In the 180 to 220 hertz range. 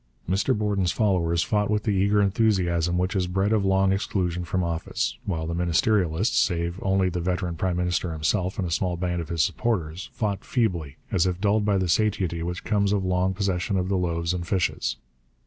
No: very low, 90 Hz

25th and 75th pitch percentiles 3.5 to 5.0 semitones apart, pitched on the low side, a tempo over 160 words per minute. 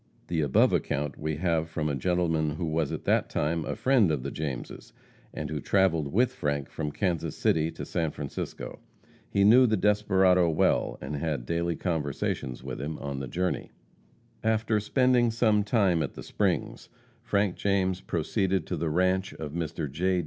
Yes: average, 4.5 semitones; very low, 85 Hz; average, 175 wpm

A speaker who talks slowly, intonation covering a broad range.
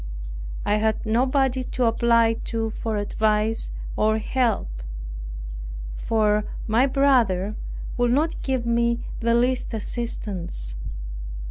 No: slow, 105 wpm; narrow, 2.5 semitones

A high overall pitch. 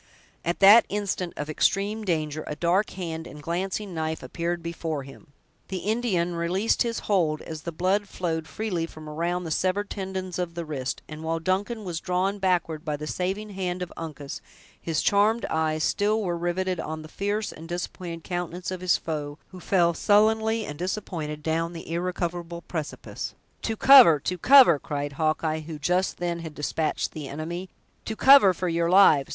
No: medium, 175 Hz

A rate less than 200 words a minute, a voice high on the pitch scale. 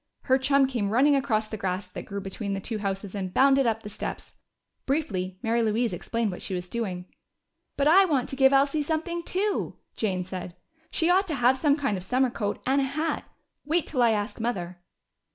No: fast, 205 wpm; high, 235 Hz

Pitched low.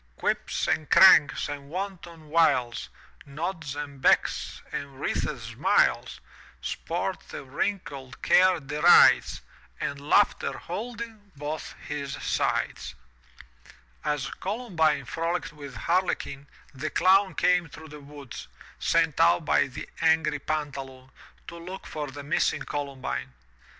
No: medium, 150 Hz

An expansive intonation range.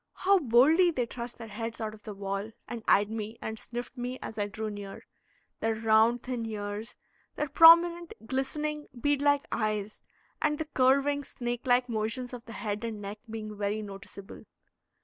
No: average, 3.9 semitones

